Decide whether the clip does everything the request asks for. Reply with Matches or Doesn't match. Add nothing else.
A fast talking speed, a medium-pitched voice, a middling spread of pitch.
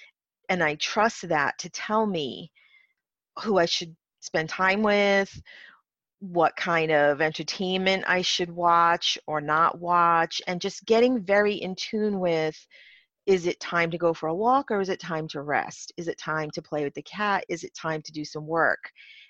Doesn't match